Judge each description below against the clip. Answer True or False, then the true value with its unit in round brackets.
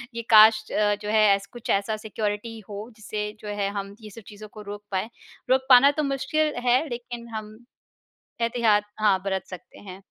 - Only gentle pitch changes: True (2.3 semitones)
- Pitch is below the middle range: False (215 Hz)